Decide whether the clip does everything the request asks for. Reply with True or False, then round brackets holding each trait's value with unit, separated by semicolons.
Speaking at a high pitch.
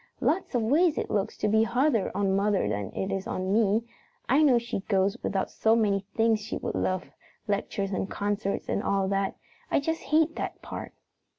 True (210 Hz)